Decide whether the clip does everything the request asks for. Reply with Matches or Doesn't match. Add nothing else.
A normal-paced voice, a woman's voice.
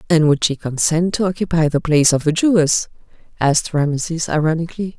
Matches